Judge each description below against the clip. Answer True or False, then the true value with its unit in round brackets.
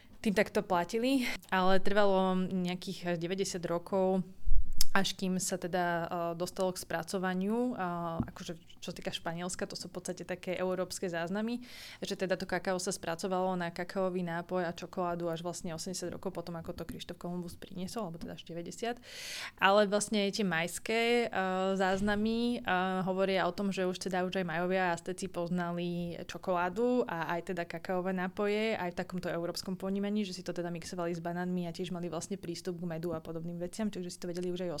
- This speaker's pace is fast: True (180 wpm)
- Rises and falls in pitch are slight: True (1.8 semitones)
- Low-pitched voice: False (185 Hz)